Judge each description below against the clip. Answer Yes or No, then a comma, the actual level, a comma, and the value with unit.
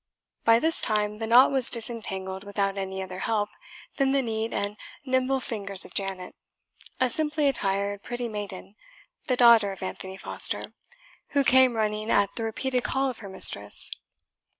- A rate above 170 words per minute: No, average, 160 wpm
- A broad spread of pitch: No, average, 4.2 semitones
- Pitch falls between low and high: No, high, 220 Hz